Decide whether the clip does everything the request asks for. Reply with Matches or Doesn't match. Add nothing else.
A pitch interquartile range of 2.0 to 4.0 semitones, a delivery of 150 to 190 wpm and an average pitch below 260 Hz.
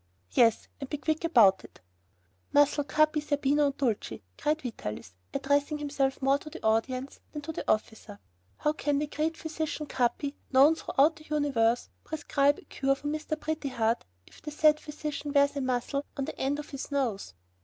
Doesn't match